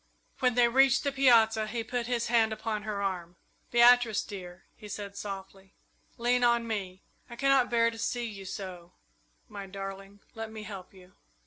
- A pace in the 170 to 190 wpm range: Yes, average, 175 wpm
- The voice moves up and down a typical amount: Yes, average, 3.4 semitones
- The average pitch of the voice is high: Yes, high, 220 Hz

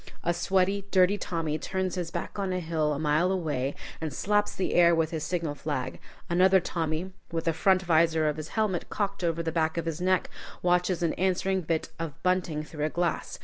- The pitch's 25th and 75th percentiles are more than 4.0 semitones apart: No, average, 2.7 semitones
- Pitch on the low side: No, medium, 170 Hz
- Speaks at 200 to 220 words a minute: Yes, fast, 205 wpm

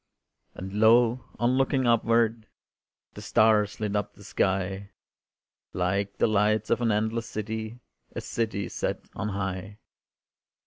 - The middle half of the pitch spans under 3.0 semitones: Yes, narrow, 2.4 semitones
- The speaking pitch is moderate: No, low, 110 Hz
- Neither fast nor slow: No, slow, 130 wpm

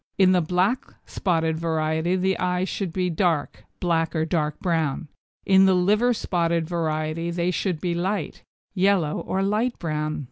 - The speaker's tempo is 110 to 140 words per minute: No, average, 155 wpm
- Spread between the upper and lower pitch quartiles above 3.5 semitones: No, average, 2.8 semitones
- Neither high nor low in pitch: Yes, medium, 175 Hz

